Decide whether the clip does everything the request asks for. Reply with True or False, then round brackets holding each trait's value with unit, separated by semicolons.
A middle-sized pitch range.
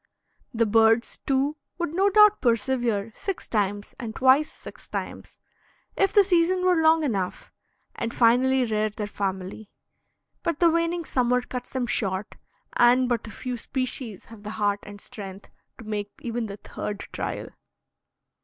False (5.7 semitones)